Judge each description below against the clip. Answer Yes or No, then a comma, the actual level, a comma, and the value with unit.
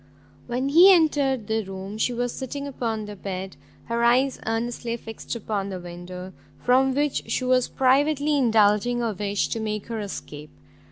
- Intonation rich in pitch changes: No, average, 4.3 semitones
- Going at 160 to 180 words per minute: Yes, average, 165 wpm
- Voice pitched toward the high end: Yes, high, 235 Hz